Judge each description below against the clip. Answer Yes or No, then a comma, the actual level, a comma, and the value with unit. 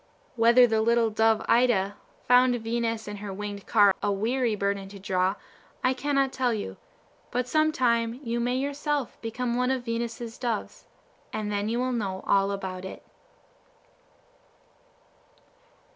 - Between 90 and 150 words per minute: Yes, average, 145 wpm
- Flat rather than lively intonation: No, average, 3.4 semitones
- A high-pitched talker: Yes, high, 230 Hz